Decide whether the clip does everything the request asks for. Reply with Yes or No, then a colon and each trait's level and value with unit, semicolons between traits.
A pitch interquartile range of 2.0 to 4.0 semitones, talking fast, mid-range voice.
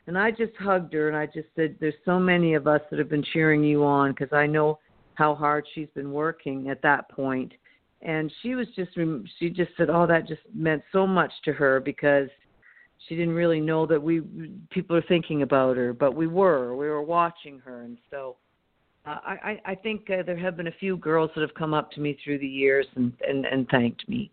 Yes: average, 3.2 semitones; fast, 225 wpm; medium, 155 Hz